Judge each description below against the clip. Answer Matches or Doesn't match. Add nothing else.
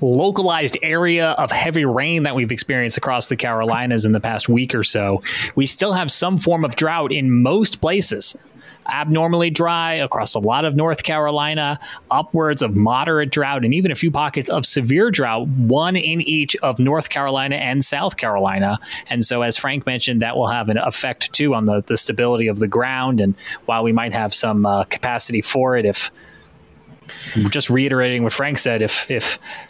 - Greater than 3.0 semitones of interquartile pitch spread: Matches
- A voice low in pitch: Matches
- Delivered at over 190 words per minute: Doesn't match